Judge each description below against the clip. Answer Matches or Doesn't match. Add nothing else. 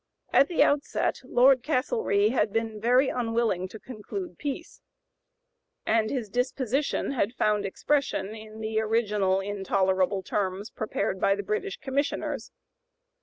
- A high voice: Matches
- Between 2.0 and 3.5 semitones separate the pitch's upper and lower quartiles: Doesn't match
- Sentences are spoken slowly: Matches